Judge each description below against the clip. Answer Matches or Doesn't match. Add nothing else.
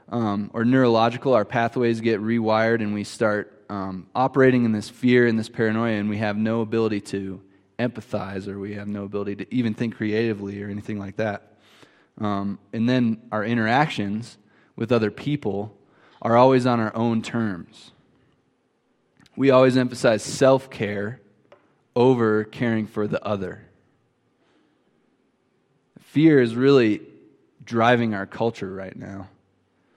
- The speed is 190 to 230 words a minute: Doesn't match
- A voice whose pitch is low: Matches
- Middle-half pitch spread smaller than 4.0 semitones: Matches